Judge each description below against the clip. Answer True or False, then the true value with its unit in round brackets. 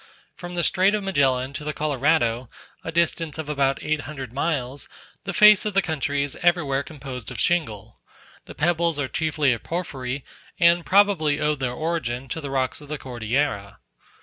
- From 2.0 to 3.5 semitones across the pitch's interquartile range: False (4.2 semitones)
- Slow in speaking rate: False (175 wpm)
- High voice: False (150 Hz)